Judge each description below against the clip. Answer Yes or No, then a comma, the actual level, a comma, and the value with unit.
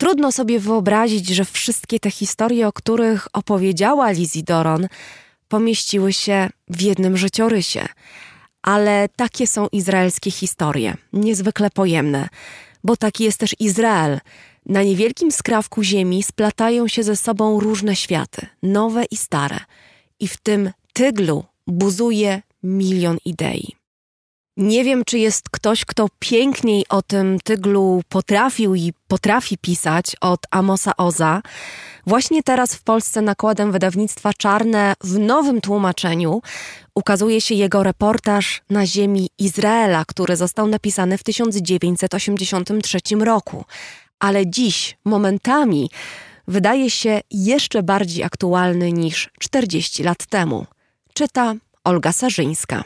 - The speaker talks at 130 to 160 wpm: No, average, 120 wpm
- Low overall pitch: No, high, 205 Hz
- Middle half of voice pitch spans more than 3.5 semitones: No, average, 2.9 semitones